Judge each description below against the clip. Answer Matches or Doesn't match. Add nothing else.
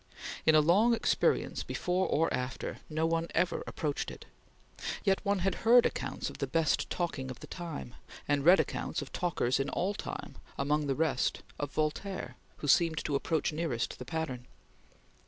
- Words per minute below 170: Doesn't match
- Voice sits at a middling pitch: Matches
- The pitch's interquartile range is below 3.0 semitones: Doesn't match